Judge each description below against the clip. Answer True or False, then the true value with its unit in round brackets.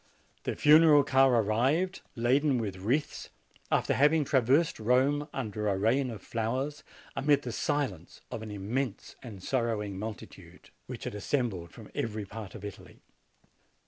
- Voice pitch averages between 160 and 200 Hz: False (120 Hz)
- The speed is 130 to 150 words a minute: True (145 wpm)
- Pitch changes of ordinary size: True (4.9 semitones)